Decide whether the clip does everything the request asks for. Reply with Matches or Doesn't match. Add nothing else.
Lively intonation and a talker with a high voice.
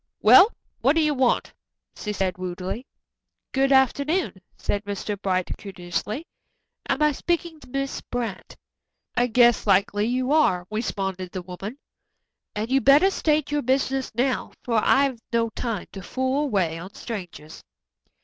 Matches